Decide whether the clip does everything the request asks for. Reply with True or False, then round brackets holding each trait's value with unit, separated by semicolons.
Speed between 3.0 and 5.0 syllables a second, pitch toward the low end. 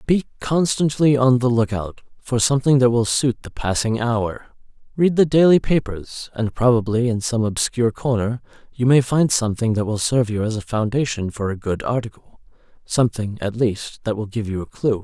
False (5.3 syllables/s; 120 Hz)